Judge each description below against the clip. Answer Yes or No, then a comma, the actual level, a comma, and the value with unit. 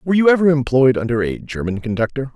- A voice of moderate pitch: No, low, 130 Hz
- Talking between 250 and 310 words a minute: No, fast, 205 wpm